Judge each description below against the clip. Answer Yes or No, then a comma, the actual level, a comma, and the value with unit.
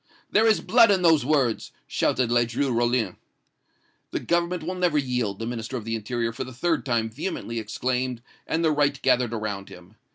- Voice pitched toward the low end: Yes, low, 125 Hz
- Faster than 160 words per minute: Yes, average, 185 wpm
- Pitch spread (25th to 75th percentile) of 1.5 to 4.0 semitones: No, average, 5.3 semitones